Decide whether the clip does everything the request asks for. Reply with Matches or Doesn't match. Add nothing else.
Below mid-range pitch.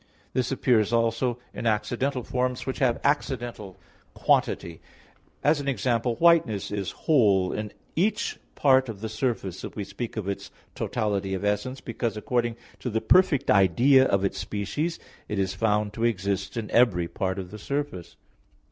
Matches